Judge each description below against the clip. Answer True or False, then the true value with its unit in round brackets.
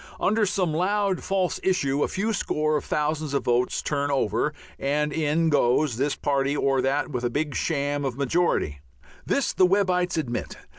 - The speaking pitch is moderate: True (150 Hz)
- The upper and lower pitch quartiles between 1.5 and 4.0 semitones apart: False (4.4 semitones)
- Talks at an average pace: True (165 wpm)